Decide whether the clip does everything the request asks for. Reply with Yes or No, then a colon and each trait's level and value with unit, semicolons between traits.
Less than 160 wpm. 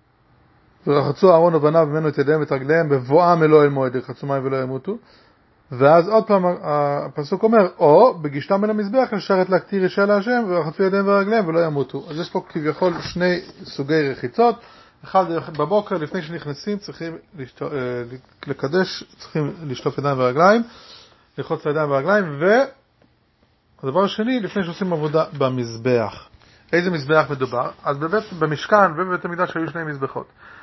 Yes: average, 140 wpm